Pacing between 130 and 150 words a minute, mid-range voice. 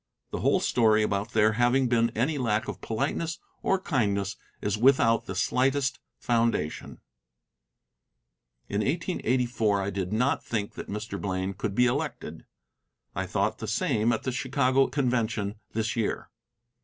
No: average, 145 wpm; low, 115 Hz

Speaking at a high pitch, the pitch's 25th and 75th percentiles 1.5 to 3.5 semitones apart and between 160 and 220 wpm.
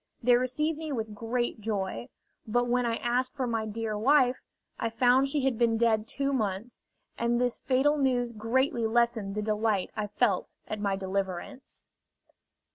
Yes: high, 235 Hz; average, 3.0 semitones; average, 165 wpm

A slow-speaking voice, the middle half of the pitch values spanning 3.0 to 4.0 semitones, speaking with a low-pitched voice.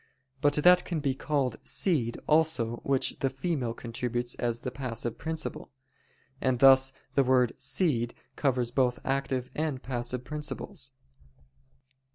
Yes: slow, 130 wpm; average, 3.4 semitones; low, 130 Hz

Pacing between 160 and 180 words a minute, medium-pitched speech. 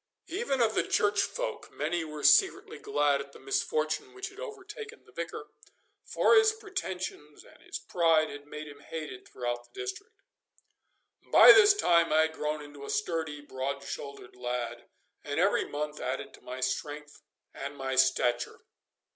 Yes: average, 165 wpm; medium, 150 Hz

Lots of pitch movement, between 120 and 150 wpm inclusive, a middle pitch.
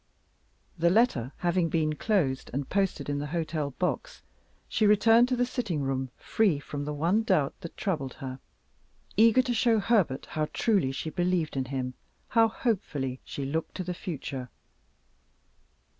No: wide, 7.3 semitones; average, 160 wpm; medium, 165 Hz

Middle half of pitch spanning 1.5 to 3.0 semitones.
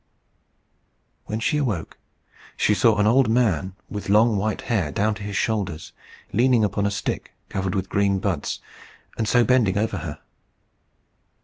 Yes: average, 2.7 semitones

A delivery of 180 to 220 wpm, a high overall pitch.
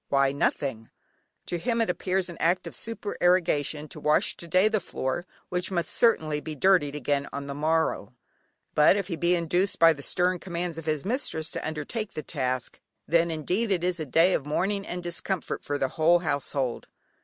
No: average, 190 wpm; medium, 170 Hz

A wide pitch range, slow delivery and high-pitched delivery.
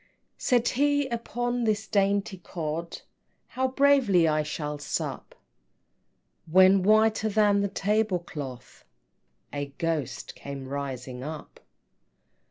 Yes: wide, 6.5 semitones; slow, 105 wpm; high, 195 Hz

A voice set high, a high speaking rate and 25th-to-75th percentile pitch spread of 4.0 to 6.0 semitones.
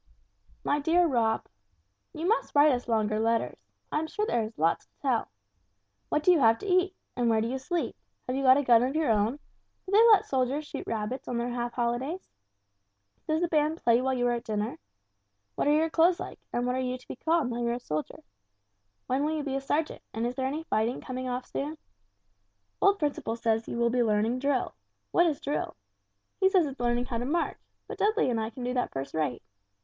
Yes: very high, 255 Hz; fast, 225 wpm; average, 4.6 semitones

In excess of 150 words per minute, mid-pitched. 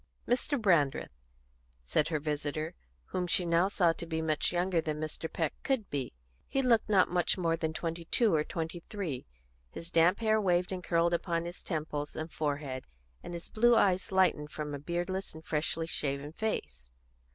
Yes: average, 180 wpm; medium, 165 Hz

